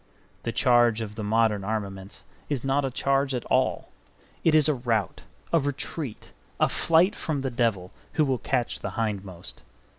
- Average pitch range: Yes, average, 4.3 semitones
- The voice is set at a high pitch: No, low, 120 Hz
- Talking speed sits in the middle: Yes, average, 170 wpm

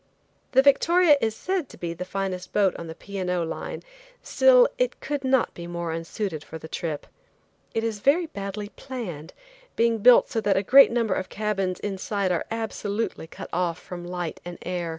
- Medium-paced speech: Yes, average, 190 wpm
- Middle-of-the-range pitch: No, high, 200 Hz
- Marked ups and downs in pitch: No, average, 4.9 semitones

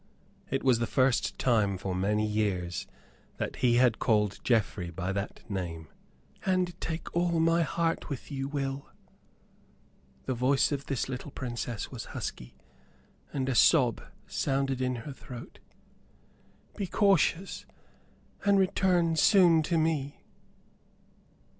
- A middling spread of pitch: No, wide, 7.0 semitones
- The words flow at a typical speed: No, slow, 130 wpm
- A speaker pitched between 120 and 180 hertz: Yes, low, 135 Hz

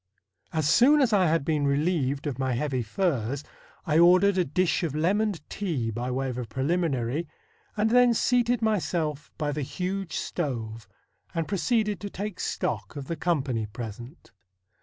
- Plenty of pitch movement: Yes, wide, 6.3 semitones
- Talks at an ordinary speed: Yes, average, 160 wpm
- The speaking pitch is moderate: Yes, medium, 155 Hz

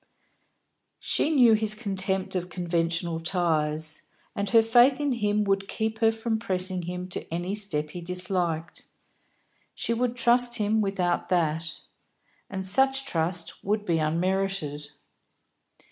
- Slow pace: Yes, slow, 130 wpm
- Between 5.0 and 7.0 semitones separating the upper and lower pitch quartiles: No, average, 4.4 semitones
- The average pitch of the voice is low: No, high, 190 Hz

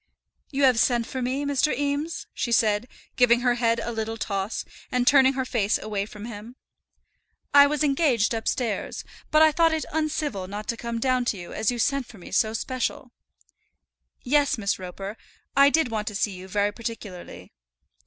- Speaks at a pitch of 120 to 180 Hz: No, high, 235 Hz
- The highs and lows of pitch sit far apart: No, average, 4.5 semitones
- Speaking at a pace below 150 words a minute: No, average, 185 wpm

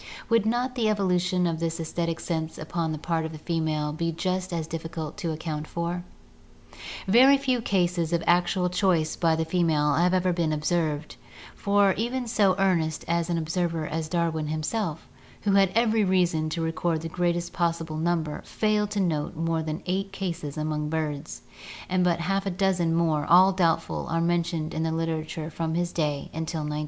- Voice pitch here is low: No, medium, 170 Hz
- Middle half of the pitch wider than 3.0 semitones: No, narrow, 2.5 semitones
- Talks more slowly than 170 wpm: No, average, 180 wpm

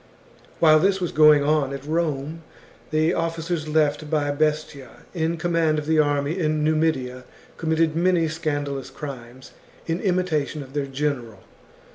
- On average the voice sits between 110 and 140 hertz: No, medium, 155 Hz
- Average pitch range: No, narrow, 2.2 semitones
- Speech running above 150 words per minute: No, average, 145 wpm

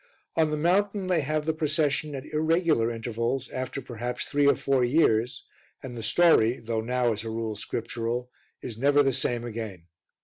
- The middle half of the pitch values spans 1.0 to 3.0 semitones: No, average, 4.7 semitones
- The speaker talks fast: No, average, 175 wpm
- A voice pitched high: No, low, 125 Hz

